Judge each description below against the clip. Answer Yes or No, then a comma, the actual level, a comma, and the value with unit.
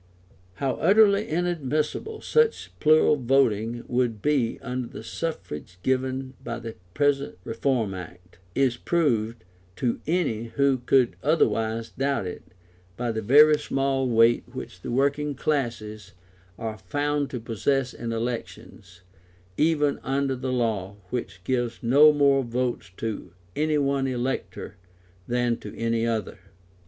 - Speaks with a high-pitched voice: No, low, 125 Hz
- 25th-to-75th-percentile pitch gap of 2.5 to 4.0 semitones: Yes, average, 3.7 semitones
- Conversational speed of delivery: No, slow, 130 wpm